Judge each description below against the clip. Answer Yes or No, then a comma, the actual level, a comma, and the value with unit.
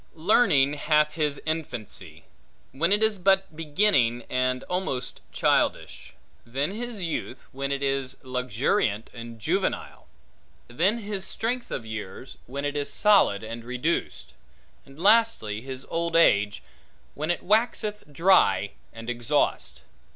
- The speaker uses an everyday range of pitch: No, wide, 7.6 semitones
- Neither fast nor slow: No, slow, 130 wpm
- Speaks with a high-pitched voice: No, medium, 140 Hz